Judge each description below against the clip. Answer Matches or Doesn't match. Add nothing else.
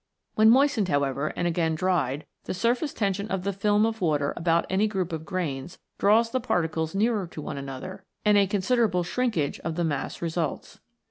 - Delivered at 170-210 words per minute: Matches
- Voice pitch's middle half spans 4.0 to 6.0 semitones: Matches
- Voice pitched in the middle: Matches